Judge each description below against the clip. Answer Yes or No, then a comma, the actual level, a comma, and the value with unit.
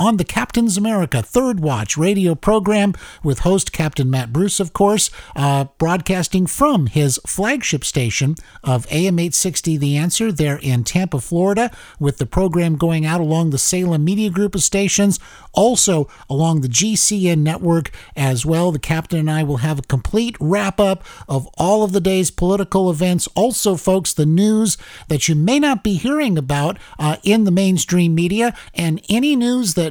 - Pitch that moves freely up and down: No, average, 4.7 semitones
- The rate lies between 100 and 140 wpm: No, average, 175 wpm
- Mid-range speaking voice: Yes, medium, 175 Hz